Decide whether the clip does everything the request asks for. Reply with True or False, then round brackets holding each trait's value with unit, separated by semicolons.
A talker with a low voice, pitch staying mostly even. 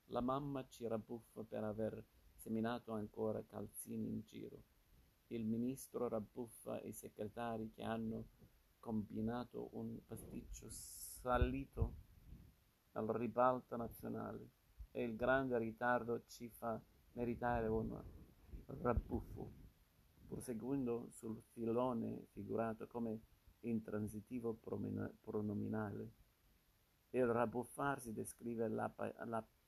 True (115 Hz; 1.7 semitones)